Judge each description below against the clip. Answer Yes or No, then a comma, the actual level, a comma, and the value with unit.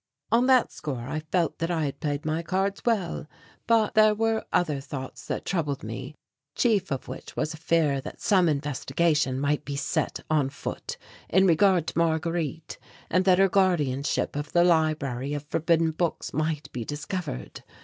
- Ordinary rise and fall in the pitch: Yes, average, 4.0 semitones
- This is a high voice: No, medium, 160 Hz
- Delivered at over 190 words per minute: No, average, 170 wpm